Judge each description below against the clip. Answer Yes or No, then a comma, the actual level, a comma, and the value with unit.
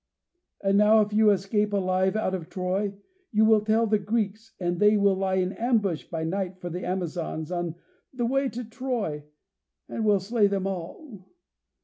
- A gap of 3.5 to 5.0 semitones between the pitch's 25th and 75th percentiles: No, average, 2.9 semitones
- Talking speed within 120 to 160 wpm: No, average, 175 wpm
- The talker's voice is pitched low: No, high, 200 Hz